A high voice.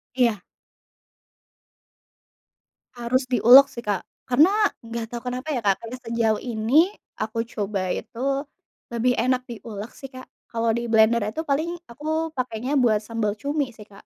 Yes: high, 235 Hz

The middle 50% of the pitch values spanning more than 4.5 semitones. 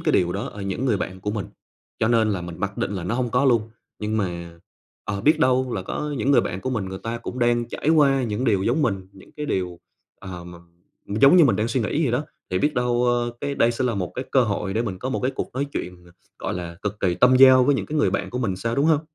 Yes: average, 5.2 semitones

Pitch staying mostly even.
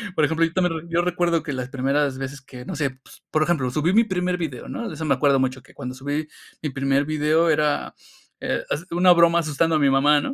No: average, 3.6 semitones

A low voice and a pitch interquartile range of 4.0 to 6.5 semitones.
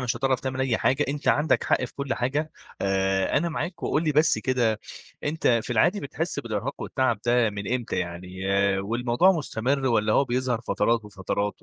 Yes: low, 125 Hz; average, 4.5 semitones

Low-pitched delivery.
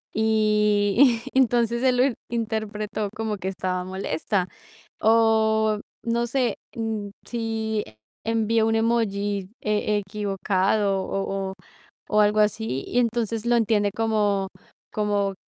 No: high, 215 Hz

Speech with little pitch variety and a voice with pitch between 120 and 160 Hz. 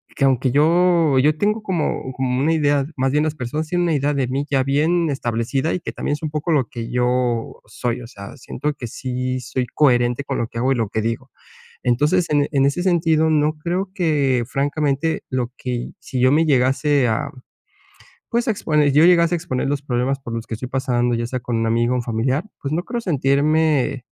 No: average, 3.8 semitones; low, 135 Hz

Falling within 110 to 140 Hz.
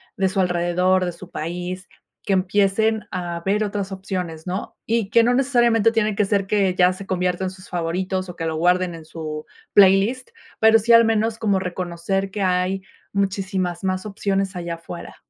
No: high, 190 Hz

